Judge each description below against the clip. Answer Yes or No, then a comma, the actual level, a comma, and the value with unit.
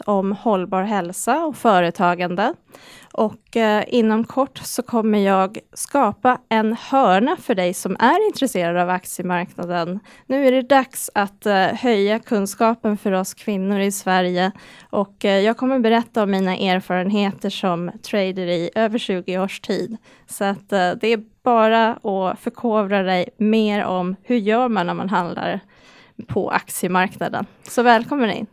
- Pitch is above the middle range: Yes, high, 205 Hz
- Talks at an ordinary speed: Yes, average, 150 wpm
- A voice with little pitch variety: No, average, 3.6 semitones